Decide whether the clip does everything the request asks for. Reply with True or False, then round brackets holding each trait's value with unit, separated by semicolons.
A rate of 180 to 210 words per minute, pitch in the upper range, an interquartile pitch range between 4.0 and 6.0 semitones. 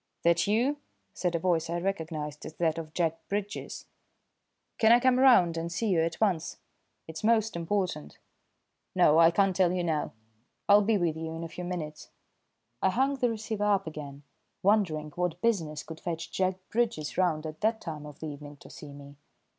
False (185 wpm; 170 Hz; 4.5 semitones)